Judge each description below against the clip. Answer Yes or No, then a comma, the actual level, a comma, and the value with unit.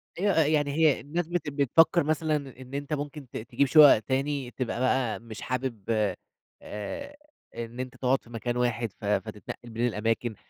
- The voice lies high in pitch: No, low, 135 Hz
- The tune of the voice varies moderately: Yes, average, 3.9 semitones